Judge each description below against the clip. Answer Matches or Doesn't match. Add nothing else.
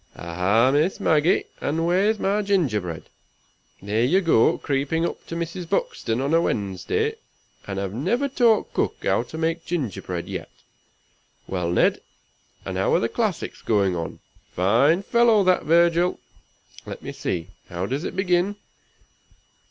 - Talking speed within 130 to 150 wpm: Matches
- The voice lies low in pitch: Doesn't match